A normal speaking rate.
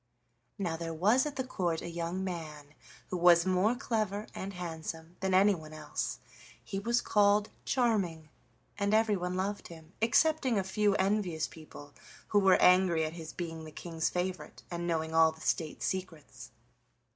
Yes: average, 160 wpm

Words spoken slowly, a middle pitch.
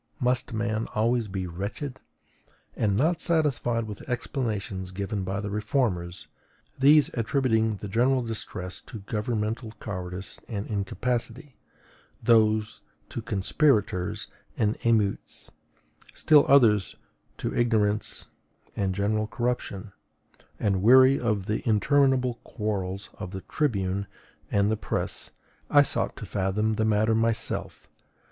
No: slow, 120 wpm; low, 110 Hz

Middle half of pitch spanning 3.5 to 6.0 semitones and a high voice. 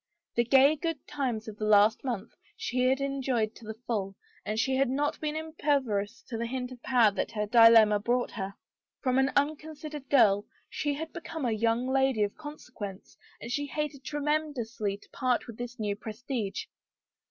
Yes: average, 4.5 semitones; very high, 250 Hz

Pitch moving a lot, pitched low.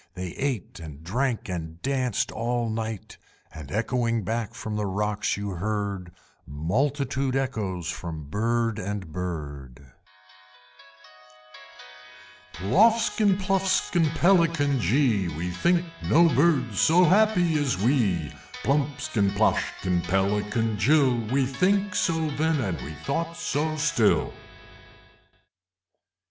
Yes: wide, 7.9 semitones; low, 115 Hz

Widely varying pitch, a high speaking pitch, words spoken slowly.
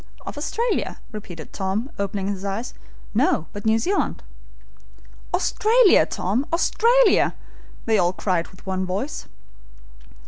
Yes: wide, 9.0 semitones; high, 210 Hz; slow, 115 wpm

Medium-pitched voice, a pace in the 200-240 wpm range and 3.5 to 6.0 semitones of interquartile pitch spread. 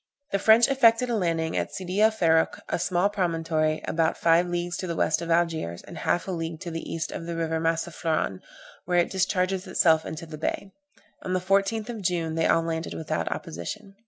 No: medium, 170 Hz; fast, 205 wpm; average, 2.8 semitones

